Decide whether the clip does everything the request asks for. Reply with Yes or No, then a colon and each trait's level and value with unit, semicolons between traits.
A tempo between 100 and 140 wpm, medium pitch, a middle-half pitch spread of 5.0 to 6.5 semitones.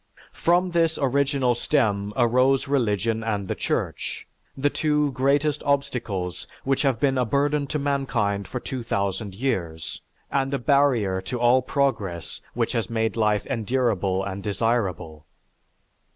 No: slow, 135 wpm; low, 120 Hz; wide, 5.4 semitones